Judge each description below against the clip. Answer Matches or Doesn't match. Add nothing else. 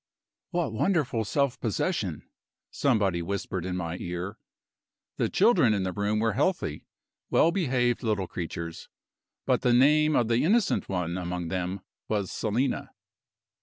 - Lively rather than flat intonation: Matches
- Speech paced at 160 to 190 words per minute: Doesn't match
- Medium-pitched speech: Doesn't match